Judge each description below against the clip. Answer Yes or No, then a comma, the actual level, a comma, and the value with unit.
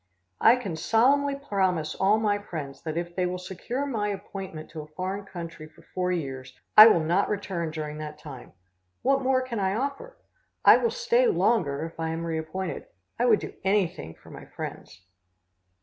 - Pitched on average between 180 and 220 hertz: Yes, medium, 185 Hz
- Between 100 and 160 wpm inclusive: No, average, 180 wpm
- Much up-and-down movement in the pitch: Yes, wide, 5.9 semitones